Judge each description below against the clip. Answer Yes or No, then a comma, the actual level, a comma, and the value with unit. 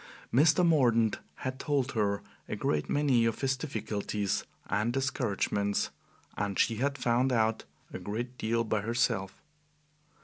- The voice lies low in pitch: Yes, low, 115 Hz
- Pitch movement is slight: No, average, 4.1 semitones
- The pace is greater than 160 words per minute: No, slow, 135 wpm